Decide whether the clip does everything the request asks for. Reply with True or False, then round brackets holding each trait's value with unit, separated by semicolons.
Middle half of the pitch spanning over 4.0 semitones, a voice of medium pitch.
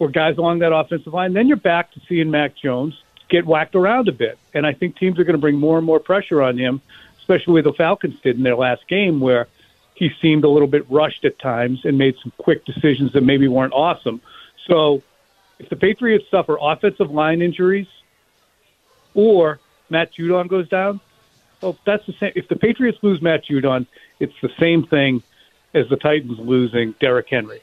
True (4.9 semitones; 155 Hz)